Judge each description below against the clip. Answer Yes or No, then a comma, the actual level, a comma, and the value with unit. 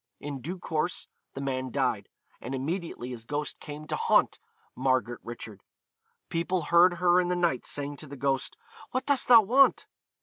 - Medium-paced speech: Yes, average, 170 wpm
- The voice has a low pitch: No, medium, 150 Hz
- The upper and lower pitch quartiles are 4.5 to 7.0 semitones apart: Yes, average, 5.2 semitones